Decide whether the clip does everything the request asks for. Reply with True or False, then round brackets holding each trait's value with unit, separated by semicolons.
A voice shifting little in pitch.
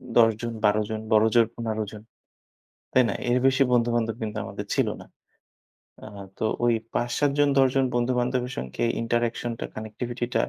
True (2.1 semitones)